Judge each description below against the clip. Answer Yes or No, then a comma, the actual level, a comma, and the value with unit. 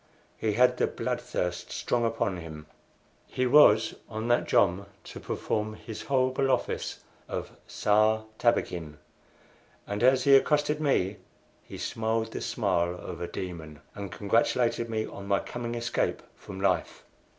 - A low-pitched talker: Yes, low, 110 Hz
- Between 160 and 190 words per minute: No, average, 145 wpm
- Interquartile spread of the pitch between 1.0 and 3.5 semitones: No, average, 4.3 semitones